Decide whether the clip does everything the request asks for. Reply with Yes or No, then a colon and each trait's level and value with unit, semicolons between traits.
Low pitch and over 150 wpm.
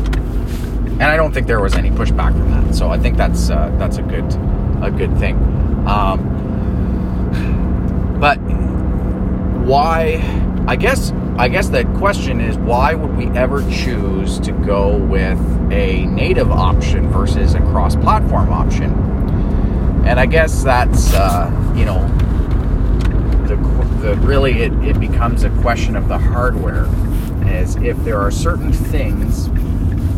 No: very low, 80 Hz; slow, 135 wpm